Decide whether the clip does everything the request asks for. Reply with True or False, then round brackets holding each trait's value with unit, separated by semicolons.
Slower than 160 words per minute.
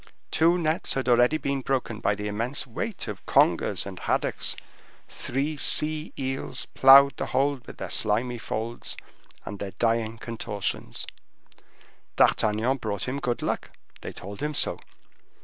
True (145 wpm)